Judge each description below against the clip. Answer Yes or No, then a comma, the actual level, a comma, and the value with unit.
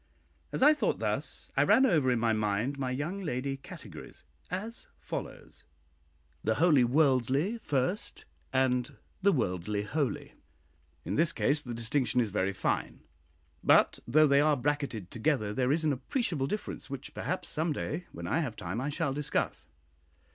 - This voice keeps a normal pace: Yes, average, 160 wpm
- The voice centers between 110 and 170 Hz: Yes, low, 135 Hz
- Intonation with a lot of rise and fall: No, average, 4.8 semitones